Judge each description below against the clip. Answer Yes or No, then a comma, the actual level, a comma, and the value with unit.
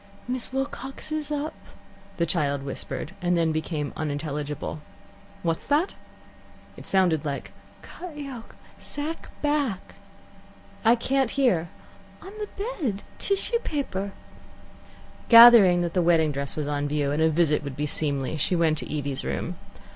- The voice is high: No, medium, 180 Hz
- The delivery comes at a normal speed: Yes, average, 160 wpm